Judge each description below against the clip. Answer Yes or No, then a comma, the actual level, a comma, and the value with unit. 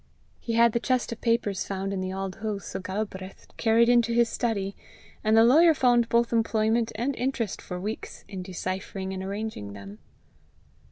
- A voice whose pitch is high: Yes, high, 220 Hz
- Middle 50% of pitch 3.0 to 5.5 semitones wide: Yes, average, 3.5 semitones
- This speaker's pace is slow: No, average, 175 wpm